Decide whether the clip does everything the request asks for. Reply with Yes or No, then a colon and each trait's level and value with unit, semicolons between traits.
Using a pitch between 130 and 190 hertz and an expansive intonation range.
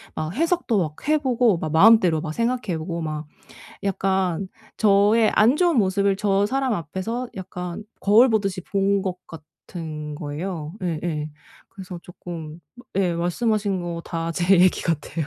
No: medium, 185 Hz; average, 4.2 semitones